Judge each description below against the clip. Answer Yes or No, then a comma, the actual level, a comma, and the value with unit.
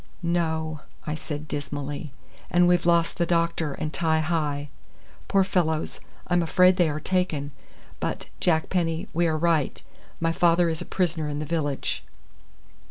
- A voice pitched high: No, medium, 160 Hz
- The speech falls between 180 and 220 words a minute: No, average, 155 wpm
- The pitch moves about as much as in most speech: No, narrow, 2.1 semitones